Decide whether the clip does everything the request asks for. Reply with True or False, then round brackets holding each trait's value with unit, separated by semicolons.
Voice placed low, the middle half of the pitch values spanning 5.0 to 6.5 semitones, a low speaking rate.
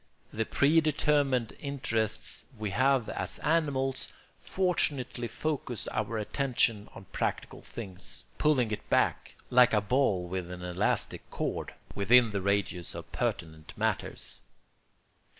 True (115 Hz; 5.3 semitones; 115 wpm)